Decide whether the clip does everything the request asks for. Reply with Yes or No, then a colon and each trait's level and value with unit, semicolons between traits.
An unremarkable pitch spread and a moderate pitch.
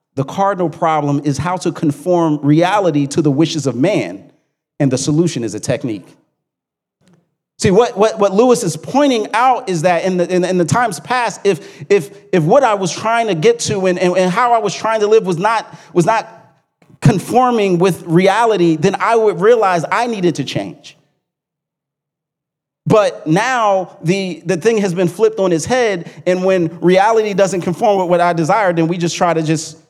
Yes: average, 4.0 semitones; medium, 180 Hz